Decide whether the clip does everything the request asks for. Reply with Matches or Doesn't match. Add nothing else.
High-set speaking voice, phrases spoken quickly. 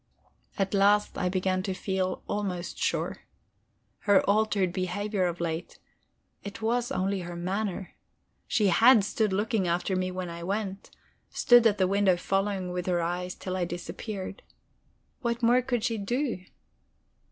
Doesn't match